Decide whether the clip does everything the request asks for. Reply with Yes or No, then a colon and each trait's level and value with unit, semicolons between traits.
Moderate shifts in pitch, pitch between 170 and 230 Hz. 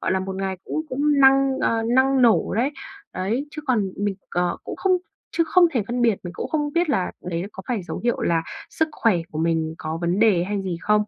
No: wide, 6.5 semitones; high, 215 Hz